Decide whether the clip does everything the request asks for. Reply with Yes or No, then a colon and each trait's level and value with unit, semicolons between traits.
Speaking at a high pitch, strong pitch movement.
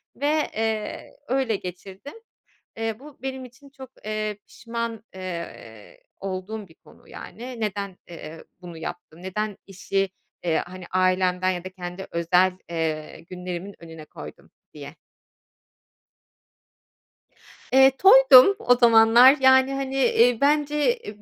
Yes: high, 210 Hz; wide, 6.1 semitones